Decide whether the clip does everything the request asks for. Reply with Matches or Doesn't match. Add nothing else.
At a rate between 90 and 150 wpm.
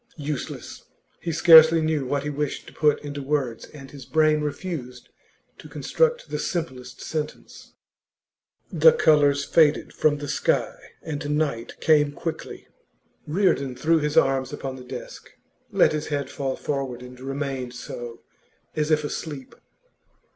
Matches